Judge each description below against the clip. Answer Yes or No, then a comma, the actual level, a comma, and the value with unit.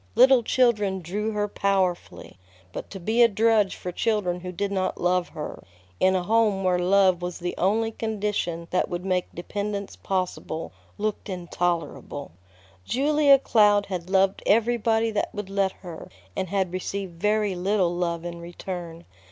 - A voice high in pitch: Yes, high, 195 Hz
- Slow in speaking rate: No, average, 155 wpm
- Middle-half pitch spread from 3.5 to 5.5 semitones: No, average, 2.9 semitones